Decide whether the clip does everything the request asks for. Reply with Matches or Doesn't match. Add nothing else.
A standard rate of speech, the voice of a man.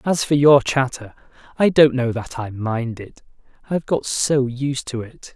Matches